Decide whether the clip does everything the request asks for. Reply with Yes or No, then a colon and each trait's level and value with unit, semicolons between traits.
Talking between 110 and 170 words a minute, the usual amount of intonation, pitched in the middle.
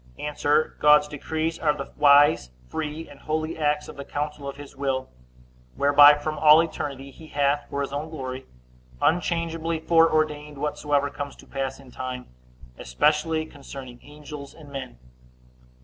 No: average, 150 wpm; narrow, 2.0 semitones; medium, 145 Hz